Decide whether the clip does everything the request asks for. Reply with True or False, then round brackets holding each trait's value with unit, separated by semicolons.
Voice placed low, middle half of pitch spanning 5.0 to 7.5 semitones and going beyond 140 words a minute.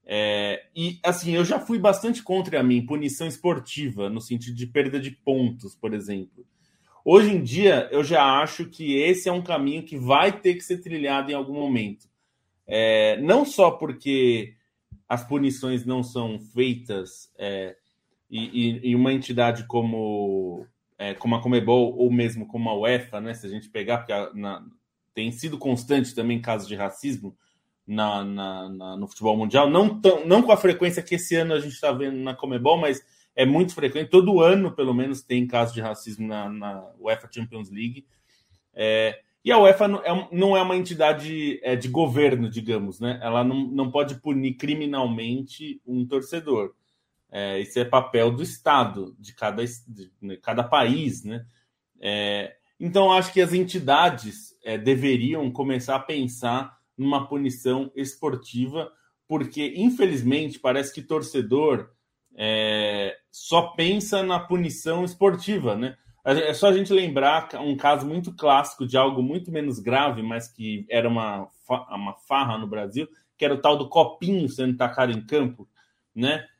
True (130 Hz; 5.3 semitones; 165 wpm)